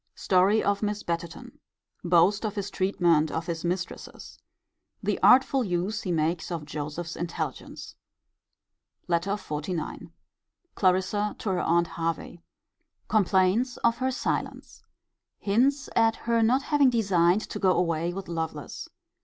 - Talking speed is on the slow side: Yes, slow, 130 wpm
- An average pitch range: Yes, average, 4.0 semitones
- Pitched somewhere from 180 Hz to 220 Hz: Yes, medium, 185 Hz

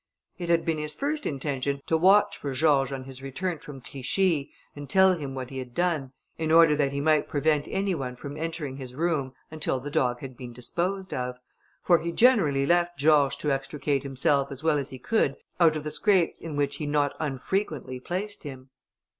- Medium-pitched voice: Yes, medium, 145 Hz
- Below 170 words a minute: No, fast, 205 wpm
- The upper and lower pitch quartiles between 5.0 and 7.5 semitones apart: No, average, 3.7 semitones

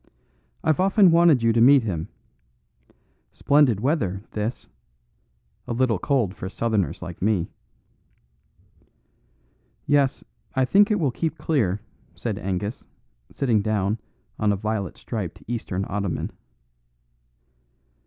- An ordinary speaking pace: No, slow, 115 wpm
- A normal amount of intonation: No, wide, 5.9 semitones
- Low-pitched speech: Yes, low, 115 Hz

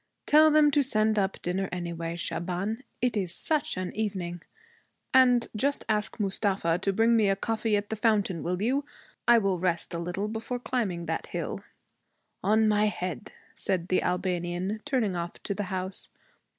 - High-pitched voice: Yes, high, 200 Hz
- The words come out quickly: No, average, 170 wpm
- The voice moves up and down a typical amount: Yes, average, 3.9 semitones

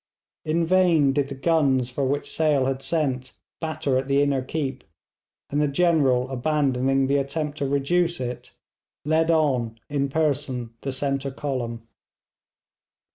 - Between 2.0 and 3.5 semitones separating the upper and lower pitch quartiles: Yes, average, 2.8 semitones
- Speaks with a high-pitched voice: No, medium, 140 Hz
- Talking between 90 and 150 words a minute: Yes, average, 140 wpm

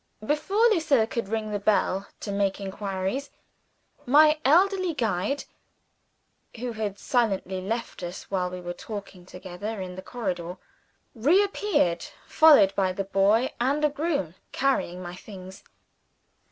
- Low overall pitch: No, high, 210 Hz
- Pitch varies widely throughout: Yes, wide, 6.7 semitones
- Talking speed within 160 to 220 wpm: No, slow, 135 wpm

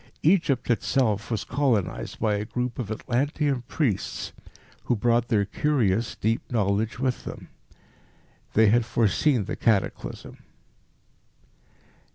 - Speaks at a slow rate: Yes, slow, 115 wpm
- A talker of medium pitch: No, low, 115 Hz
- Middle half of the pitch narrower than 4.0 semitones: Yes, average, 3.5 semitones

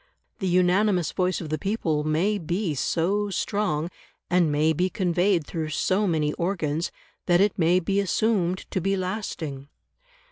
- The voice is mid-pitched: Yes, medium, 180 Hz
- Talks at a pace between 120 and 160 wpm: Yes, average, 150 wpm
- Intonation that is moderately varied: Yes, average, 3.6 semitones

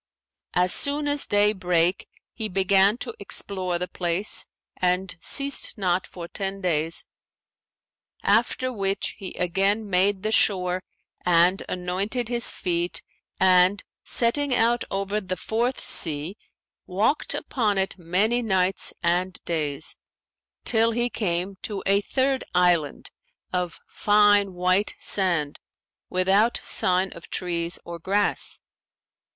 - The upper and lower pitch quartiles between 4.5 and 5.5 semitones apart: No, average, 2.9 semitones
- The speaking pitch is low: No, high, 190 Hz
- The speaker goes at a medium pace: No, slow, 120 wpm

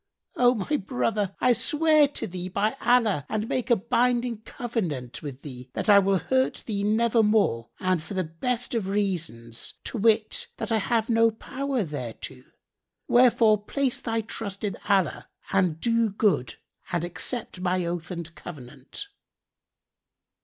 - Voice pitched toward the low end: No, high, 210 Hz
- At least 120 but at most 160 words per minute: Yes, average, 150 wpm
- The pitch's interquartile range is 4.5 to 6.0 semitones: Yes, average, 5.1 semitones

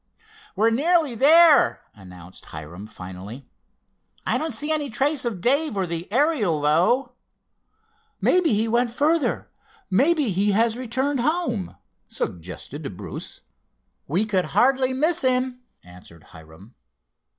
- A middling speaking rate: No, slow, 115 wpm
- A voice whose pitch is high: Yes, high, 235 Hz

